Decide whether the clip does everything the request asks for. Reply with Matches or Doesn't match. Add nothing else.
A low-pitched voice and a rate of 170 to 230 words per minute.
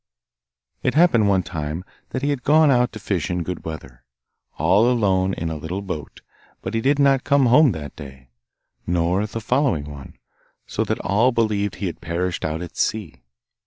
Matches